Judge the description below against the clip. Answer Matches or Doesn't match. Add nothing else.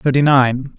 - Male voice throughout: Matches